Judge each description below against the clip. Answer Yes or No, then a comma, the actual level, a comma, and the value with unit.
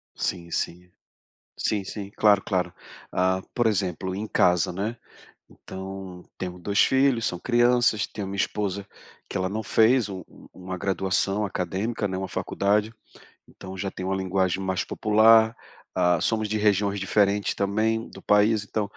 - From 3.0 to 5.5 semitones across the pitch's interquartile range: No, narrow, 2.4 semitones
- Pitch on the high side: No, low, 100 Hz